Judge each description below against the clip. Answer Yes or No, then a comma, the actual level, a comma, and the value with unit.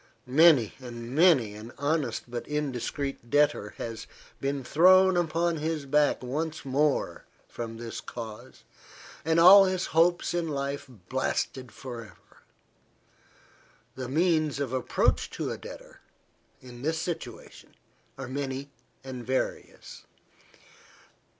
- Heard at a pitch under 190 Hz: Yes, medium, 140 Hz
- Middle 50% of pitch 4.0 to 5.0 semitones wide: Yes, average, 4.6 semitones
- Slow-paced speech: Yes, slow, 120 wpm